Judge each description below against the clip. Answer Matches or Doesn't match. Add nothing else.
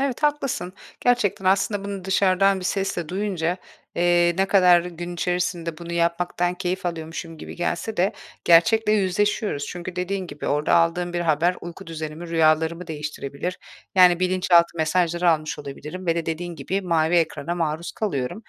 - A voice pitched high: Doesn't match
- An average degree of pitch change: Doesn't match